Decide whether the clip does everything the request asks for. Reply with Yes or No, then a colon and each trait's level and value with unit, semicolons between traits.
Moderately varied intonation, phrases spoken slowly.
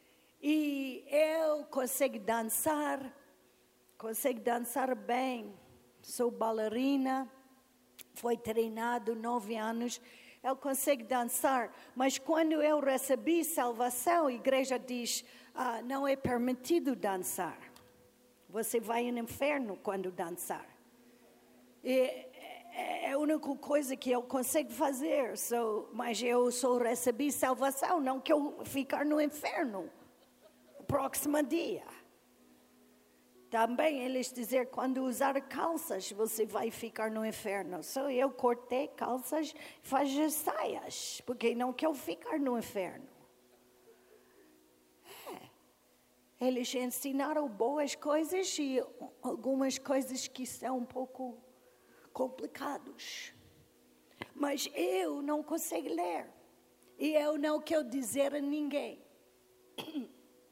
Yes: average, 3.7 semitones; slow, 105 wpm